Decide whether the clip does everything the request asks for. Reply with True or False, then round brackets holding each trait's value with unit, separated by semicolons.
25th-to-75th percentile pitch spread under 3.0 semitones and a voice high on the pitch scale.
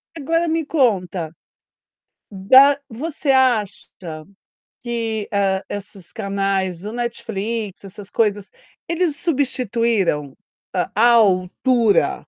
False (5.0 semitones; 220 Hz)